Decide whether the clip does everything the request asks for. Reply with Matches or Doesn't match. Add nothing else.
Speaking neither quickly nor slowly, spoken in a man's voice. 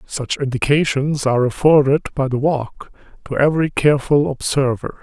Doesn't match